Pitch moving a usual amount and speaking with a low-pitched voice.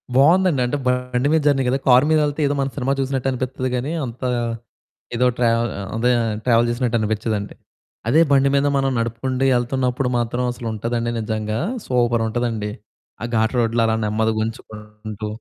Yes: average, 3.0 semitones; low, 120 Hz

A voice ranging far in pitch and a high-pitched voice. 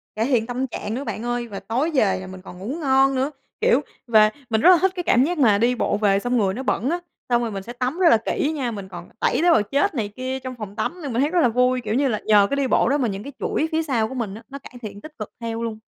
No: average, 4.3 semitones; high, 245 Hz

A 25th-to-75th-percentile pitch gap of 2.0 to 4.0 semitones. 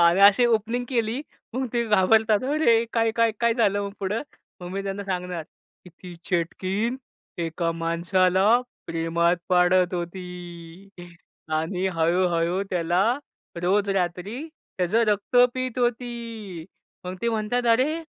No: average, 4.5 semitones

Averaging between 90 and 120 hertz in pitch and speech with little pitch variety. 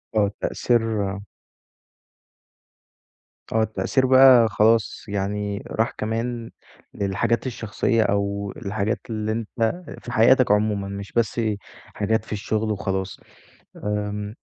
Yes: low, 110 Hz; narrow, 2.2 semitones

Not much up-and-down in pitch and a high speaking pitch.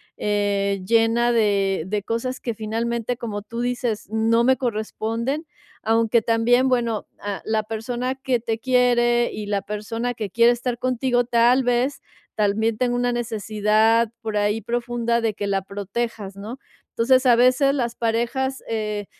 Yes: narrow, 2.2 semitones; high, 230 Hz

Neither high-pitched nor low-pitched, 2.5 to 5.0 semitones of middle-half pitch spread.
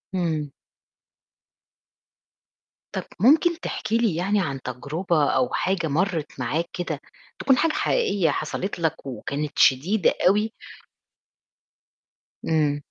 No: medium, 170 Hz; wide, 5.6 semitones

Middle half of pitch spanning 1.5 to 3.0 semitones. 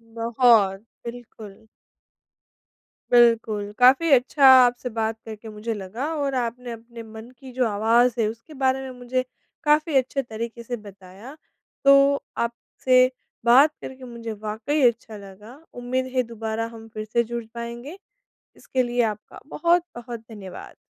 Yes: narrow, 2.6 semitones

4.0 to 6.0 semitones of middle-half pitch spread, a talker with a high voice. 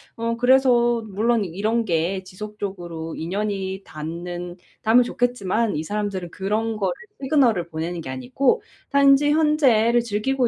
Yes: average, 5.2 semitones; high, 210 Hz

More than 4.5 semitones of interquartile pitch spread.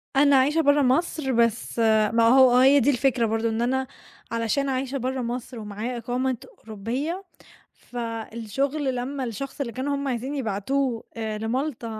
No: average, 3.1 semitones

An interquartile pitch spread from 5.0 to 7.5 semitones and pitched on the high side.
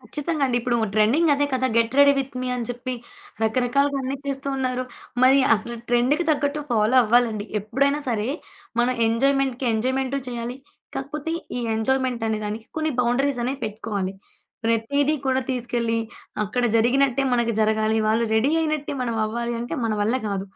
No: average, 3.3 semitones; high, 245 Hz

